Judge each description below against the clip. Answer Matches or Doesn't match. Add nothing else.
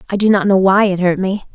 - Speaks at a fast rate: Matches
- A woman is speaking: Matches